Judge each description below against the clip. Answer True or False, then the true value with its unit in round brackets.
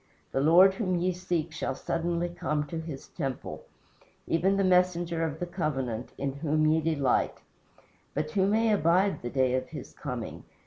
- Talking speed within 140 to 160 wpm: False (170 wpm)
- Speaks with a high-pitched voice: False (165 Hz)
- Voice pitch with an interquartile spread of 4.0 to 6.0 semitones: False (3.6 semitones)